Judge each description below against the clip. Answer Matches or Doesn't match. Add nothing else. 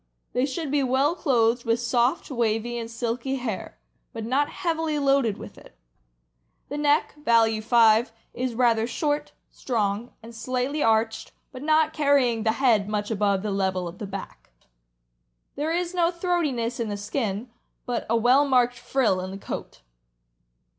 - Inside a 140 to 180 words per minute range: Matches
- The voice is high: Matches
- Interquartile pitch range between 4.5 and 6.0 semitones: Doesn't match